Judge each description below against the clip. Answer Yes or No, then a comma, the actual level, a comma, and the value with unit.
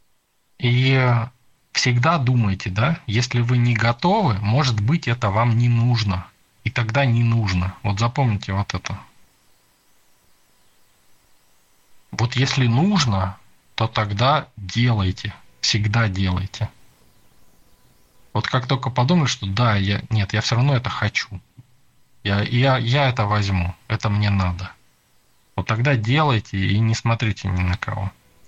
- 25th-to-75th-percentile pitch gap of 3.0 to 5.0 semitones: Yes, average, 3.7 semitones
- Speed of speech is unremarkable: Yes, average, 125 wpm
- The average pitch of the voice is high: No, low, 115 Hz